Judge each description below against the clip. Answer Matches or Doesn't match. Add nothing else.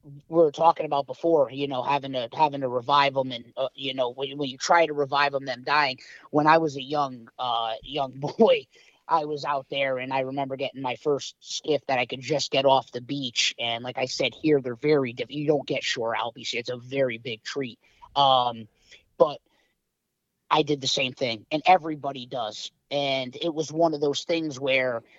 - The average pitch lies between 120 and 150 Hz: Matches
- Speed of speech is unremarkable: Doesn't match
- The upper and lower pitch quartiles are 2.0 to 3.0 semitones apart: Matches